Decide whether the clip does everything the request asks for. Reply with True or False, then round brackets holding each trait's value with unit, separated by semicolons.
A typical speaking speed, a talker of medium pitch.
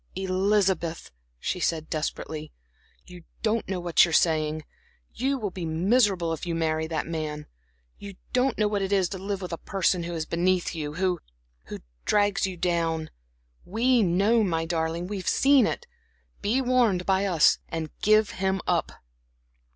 True (165 wpm; 180 Hz)